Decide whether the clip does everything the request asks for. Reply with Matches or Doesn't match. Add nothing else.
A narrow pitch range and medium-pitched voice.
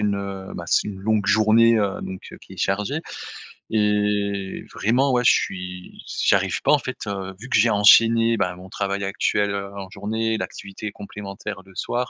Doesn't match